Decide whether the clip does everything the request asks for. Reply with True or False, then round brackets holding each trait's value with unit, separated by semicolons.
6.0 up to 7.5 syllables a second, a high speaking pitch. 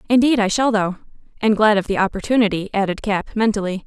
True (6.2 syllables/s; 210 Hz)